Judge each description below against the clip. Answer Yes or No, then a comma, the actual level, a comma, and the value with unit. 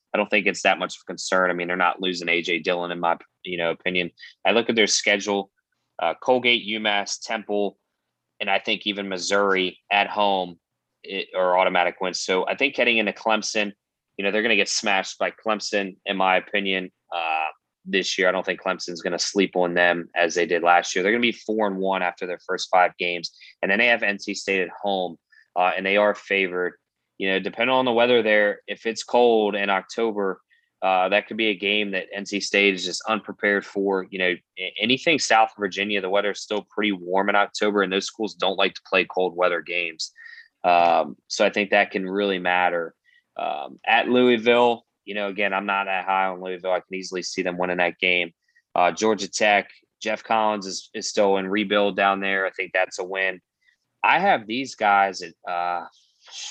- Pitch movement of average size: No, narrow, 2.2 semitones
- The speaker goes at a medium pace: No, fast, 210 wpm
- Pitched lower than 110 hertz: Yes, low, 100 Hz